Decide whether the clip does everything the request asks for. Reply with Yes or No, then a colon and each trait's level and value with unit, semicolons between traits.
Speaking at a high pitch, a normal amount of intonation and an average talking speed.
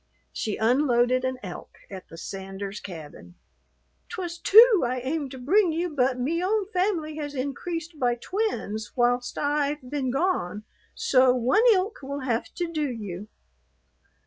No: very high, 265 Hz; wide, 5.7 semitones; average, 145 wpm